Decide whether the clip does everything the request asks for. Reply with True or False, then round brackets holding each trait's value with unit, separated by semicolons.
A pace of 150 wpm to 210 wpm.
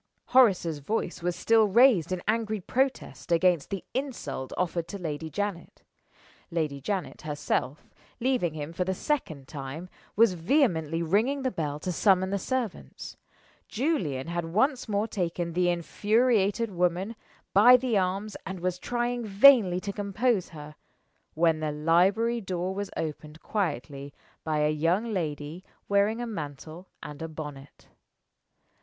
False (140 wpm)